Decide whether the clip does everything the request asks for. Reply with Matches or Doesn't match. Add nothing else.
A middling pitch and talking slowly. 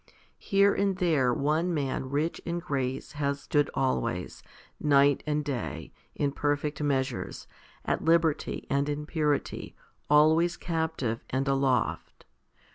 Matches